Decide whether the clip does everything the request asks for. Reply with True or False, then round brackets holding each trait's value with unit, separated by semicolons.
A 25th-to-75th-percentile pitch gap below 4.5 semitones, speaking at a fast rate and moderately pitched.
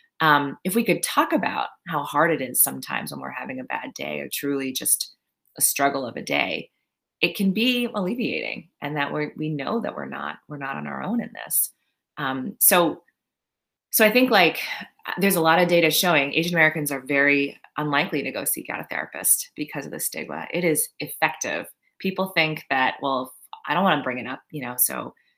False (4.9 semitones; 210 wpm; 150 Hz)